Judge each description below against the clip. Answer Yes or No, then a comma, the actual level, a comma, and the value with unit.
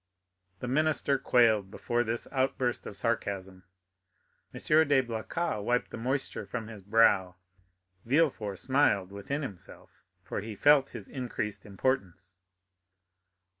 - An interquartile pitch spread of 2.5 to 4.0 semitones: No, average, 4.9 semitones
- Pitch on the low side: Yes, low, 115 Hz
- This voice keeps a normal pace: No, slow, 120 wpm